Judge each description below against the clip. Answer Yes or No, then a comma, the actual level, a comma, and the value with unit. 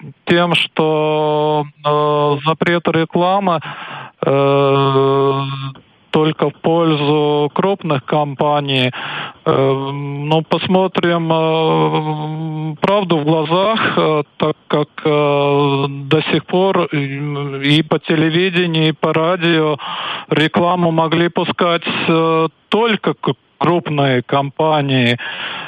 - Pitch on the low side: No, medium, 155 Hz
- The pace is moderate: No, slow, 90 wpm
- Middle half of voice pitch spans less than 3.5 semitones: Yes, average, 2.9 semitones